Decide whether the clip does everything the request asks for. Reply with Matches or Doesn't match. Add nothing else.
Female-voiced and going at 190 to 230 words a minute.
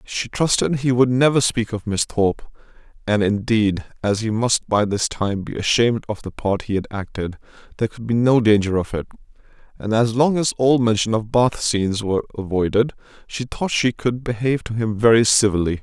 Doesn't match